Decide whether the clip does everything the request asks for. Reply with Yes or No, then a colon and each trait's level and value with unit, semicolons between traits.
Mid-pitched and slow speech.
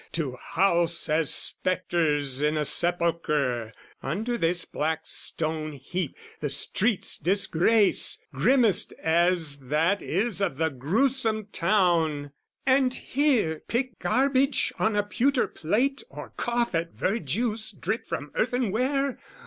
Yes: medium, 180 Hz; slow, 115 wpm